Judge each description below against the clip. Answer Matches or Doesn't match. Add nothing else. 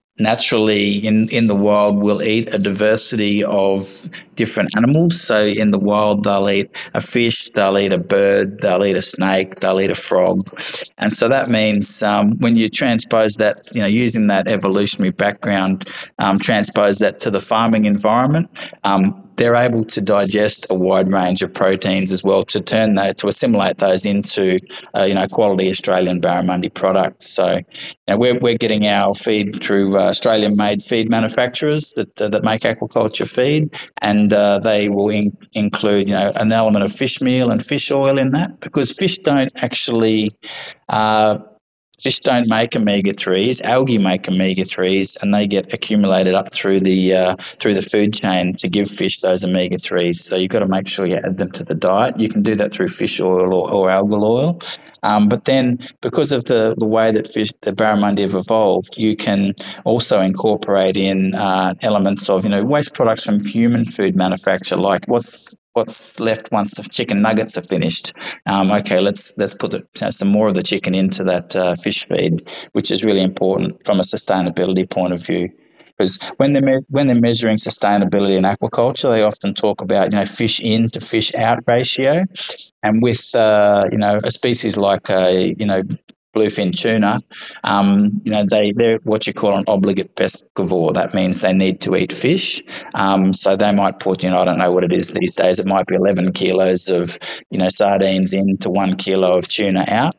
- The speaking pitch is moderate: Doesn't match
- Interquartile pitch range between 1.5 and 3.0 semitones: Matches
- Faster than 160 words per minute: Matches